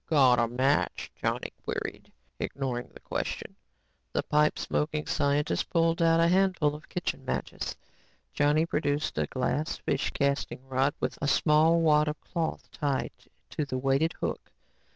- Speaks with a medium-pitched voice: Yes, medium, 150 Hz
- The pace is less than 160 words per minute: Yes, average, 150 wpm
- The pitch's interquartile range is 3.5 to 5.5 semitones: No, average, 2.9 semitones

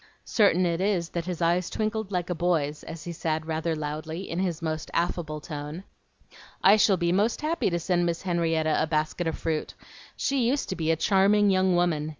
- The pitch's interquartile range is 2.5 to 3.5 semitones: Yes, average, 3.0 semitones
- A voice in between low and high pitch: Yes, medium, 170 Hz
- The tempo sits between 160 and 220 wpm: Yes, average, 200 wpm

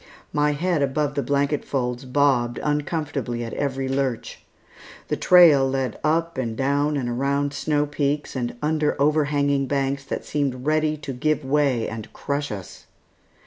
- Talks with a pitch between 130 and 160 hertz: Yes, medium, 140 Hz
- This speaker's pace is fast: No, average, 150 wpm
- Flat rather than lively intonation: Yes, narrow, 2.0 semitones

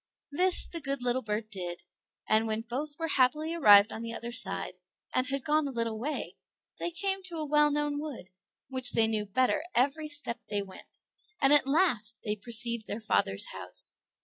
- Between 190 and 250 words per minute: Yes, average, 195 wpm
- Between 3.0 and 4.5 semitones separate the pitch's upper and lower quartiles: No, average, 5.2 semitones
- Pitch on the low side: No, very high, 255 Hz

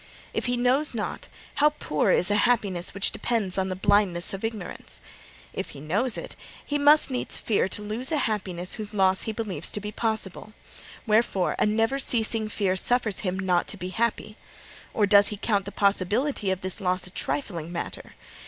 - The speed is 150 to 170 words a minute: No, average, 190 wpm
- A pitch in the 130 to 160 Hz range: No, high, 210 Hz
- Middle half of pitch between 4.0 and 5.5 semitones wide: No, average, 3.5 semitones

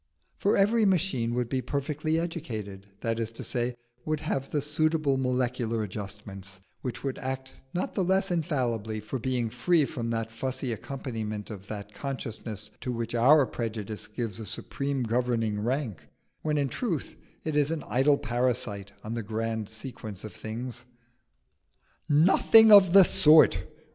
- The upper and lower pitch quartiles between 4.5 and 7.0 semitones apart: Yes, average, 4.9 semitones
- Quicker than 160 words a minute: No, average, 155 wpm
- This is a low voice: Yes, low, 125 Hz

